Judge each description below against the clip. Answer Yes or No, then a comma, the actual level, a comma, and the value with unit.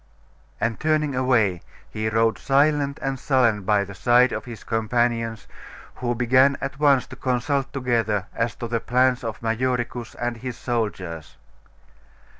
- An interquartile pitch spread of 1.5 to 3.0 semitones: Yes, narrow, 2.5 semitones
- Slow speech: No, average, 145 wpm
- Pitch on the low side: Yes, low, 120 Hz